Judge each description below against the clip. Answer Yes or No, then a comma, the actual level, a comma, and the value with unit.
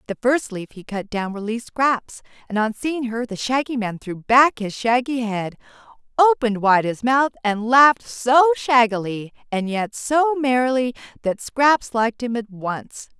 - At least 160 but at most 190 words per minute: Yes, average, 175 wpm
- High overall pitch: Yes, high, 235 Hz